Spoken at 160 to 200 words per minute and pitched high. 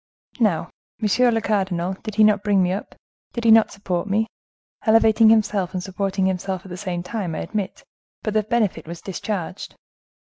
Yes: average, 175 wpm; high, 200 Hz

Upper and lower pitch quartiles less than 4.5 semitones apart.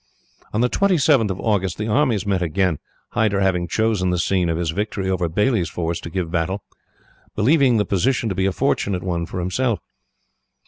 Yes: average, 3.8 semitones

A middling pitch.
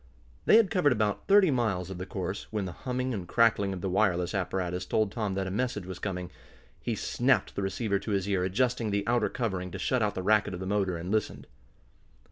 No: low, 100 Hz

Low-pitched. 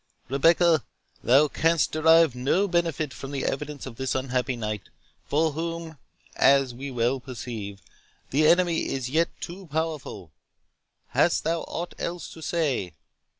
No: medium, 145 Hz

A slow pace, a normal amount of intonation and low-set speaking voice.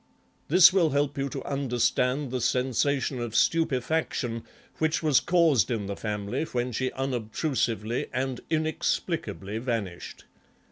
Yes: slow, 125 wpm; average, 4.2 semitones; low, 130 Hz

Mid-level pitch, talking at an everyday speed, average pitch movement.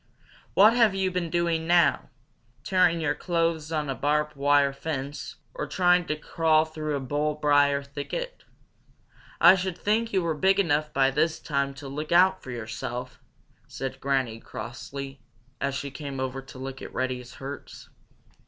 Yes: medium, 150 Hz; average, 165 wpm; average, 3.8 semitones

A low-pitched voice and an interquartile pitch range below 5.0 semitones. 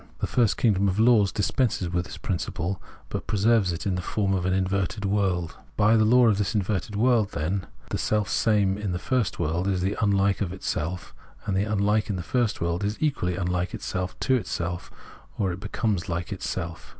Yes: low, 100 Hz; average, 2.9 semitones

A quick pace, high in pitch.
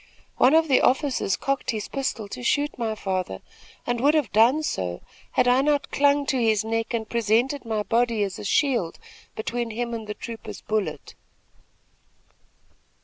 No: average, 165 wpm; high, 235 Hz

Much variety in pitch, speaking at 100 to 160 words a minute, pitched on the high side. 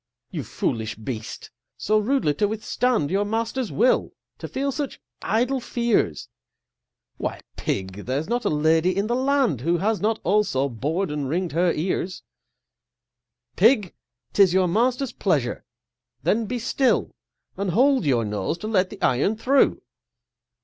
Yes: wide, 7.6 semitones; average, 145 wpm; high, 200 Hz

